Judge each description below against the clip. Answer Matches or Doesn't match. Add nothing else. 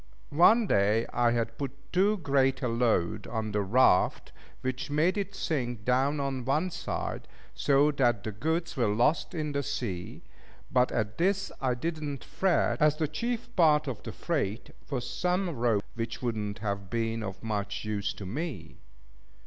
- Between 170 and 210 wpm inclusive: Matches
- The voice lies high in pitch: Doesn't match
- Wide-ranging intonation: Matches